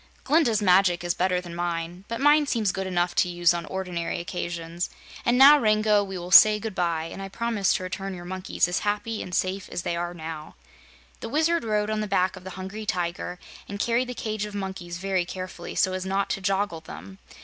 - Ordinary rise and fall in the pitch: Yes, average, 3.3 semitones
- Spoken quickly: Yes, fast, 215 wpm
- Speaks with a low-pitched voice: No, high, 190 Hz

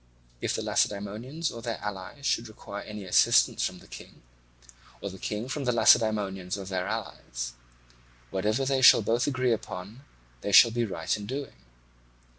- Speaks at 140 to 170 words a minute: Yes, average, 160 wpm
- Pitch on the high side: No, low, 105 Hz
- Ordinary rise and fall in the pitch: Yes, average, 4.0 semitones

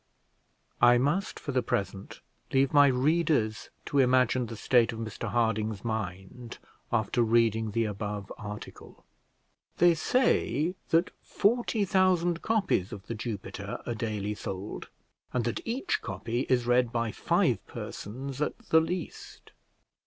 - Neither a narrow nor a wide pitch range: No, wide, 5.9 semitones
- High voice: No, low, 120 Hz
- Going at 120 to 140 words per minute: Yes, slow, 135 wpm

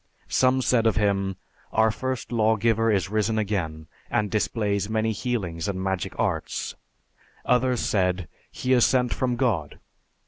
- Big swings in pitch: No, average, 3.8 semitones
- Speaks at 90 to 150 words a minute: Yes, average, 145 wpm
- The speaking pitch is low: Yes, low, 110 Hz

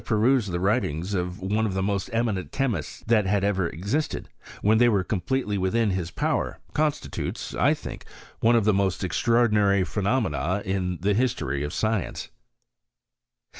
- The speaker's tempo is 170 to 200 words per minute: No, average, 160 wpm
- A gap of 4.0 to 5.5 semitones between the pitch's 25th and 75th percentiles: No, average, 3.6 semitones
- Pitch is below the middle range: Yes, low, 100 Hz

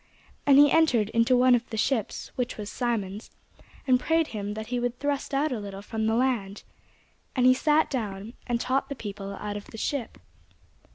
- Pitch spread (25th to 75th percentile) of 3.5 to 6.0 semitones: Yes, average, 4.0 semitones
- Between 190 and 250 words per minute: Yes, average, 195 wpm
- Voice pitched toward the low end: No, high, 240 Hz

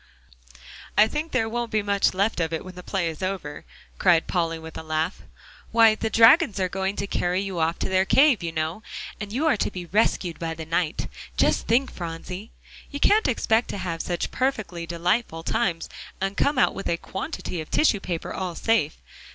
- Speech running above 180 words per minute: Yes, average, 200 wpm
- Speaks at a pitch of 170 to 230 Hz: Yes, high, 190 Hz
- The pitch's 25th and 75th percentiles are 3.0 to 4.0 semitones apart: No, average, 4.9 semitones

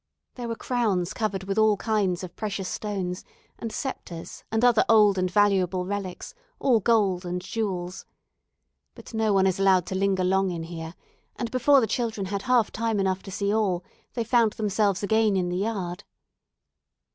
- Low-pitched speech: No, high, 200 Hz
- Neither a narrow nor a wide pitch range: Yes, average, 3.2 semitones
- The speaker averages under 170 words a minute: No, average, 175 wpm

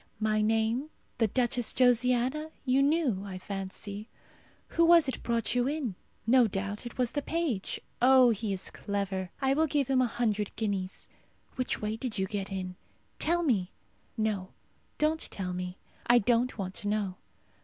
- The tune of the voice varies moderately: Yes, average, 4.5 semitones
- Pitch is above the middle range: Yes, high, 225 Hz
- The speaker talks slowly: No, average, 165 wpm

